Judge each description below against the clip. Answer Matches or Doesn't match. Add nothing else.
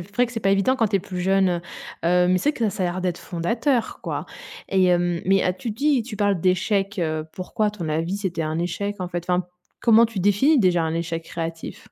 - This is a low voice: Doesn't match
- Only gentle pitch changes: Doesn't match